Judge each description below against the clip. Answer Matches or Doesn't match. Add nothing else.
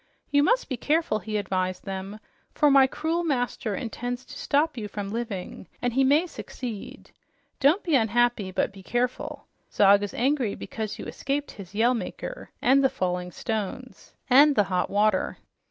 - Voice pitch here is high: Matches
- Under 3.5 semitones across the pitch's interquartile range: Doesn't match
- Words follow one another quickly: Doesn't match